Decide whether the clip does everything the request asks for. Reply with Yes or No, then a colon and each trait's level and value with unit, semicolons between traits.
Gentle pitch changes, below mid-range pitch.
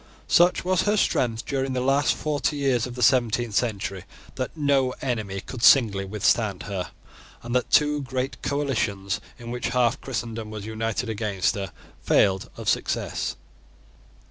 No: average, 4.1 semitones; low, 120 Hz